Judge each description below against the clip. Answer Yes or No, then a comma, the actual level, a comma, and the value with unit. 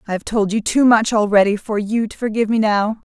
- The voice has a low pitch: No, high, 215 Hz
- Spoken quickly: Yes, fast, 250 wpm